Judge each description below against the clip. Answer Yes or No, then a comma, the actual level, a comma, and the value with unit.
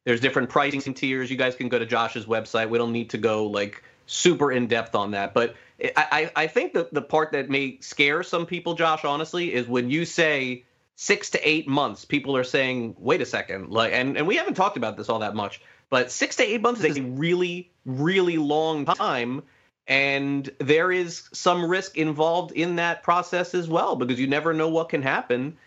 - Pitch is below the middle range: No, medium, 145 Hz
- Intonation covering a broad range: No, average, 4.9 semitones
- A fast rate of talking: Yes, fast, 210 wpm